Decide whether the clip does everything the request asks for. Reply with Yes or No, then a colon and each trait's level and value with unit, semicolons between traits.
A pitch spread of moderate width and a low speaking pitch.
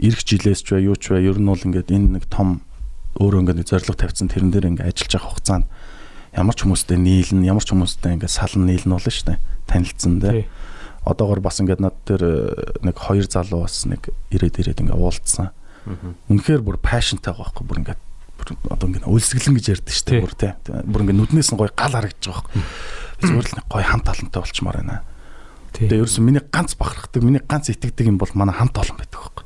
Yes: average, 3.5 semitones; low, 100 Hz